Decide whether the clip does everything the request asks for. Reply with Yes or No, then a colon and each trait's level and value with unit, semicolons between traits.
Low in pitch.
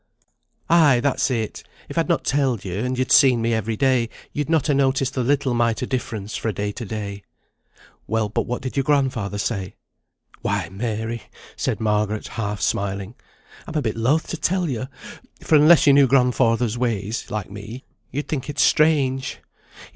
Yes: low, 120 Hz